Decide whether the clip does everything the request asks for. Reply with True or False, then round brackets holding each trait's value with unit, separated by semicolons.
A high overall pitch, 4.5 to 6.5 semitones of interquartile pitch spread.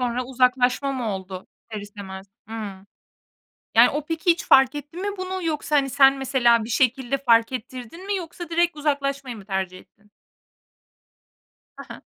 True (260 Hz; 4.9 semitones)